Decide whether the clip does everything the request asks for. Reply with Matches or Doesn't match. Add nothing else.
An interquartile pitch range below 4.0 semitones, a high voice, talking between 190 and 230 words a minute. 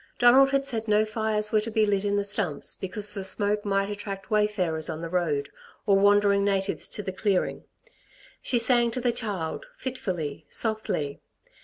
Doesn't match